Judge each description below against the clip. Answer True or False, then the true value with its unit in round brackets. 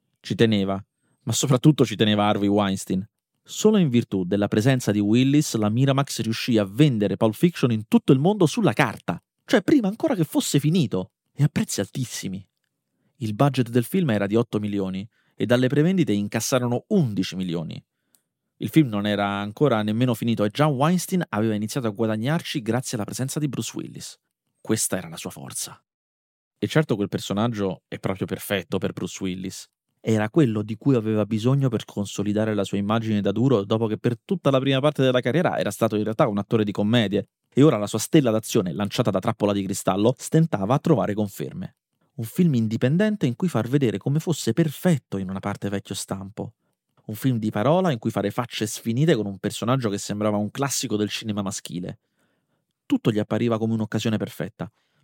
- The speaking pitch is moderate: False (115 Hz)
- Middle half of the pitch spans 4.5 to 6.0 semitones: True (5.1 semitones)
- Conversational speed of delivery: False (190 wpm)